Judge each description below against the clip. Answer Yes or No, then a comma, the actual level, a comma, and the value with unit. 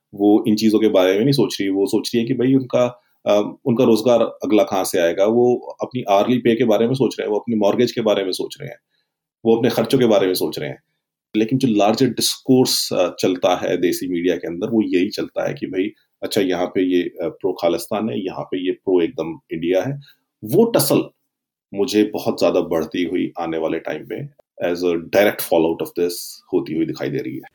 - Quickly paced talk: Yes, fast, 225 wpm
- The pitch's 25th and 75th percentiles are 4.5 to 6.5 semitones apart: No, average, 4.1 semitones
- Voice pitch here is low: Yes, low, 110 Hz